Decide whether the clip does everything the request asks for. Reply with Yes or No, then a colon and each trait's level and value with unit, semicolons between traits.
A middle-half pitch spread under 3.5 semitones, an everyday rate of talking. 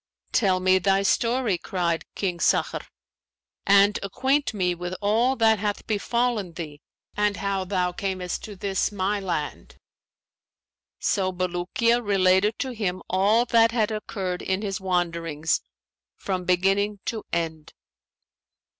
No: average, 2.9 semitones; slow, 130 wpm